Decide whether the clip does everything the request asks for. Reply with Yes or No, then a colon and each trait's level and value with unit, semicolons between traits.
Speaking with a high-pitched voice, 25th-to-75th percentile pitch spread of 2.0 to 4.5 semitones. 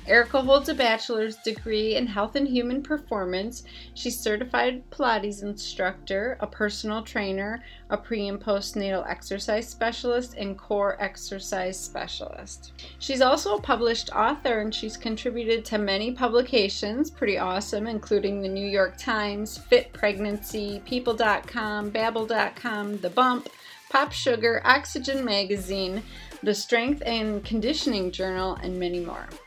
Yes: high, 215 Hz; average, 3.3 semitones